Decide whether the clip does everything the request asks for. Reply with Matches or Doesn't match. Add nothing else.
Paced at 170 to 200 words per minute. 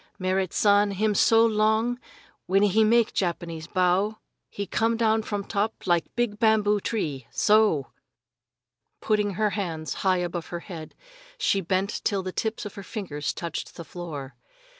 Doesn't match